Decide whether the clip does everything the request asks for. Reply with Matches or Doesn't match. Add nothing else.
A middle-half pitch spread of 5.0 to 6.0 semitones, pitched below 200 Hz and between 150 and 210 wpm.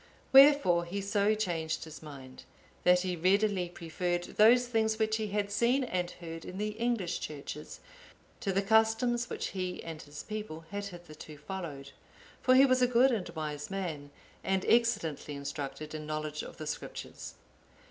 Matches